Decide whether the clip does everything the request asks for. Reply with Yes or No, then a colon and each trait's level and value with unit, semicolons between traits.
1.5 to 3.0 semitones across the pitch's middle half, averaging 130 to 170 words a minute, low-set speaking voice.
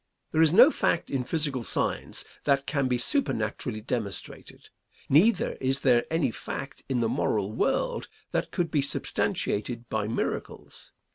No: average, 4.7 semitones; average, 145 wpm; low, 130 Hz